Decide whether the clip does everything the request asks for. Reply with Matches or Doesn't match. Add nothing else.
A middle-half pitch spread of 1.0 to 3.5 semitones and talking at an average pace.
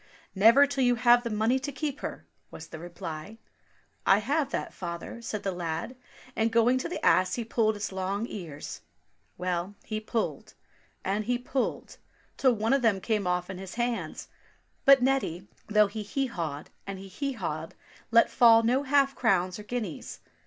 Doesn't match